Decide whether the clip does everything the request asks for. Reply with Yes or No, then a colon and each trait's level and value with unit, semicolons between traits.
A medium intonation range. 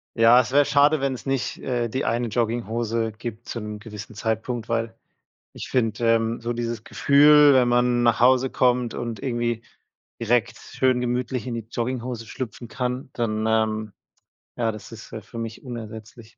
No: narrow, 1.8 semitones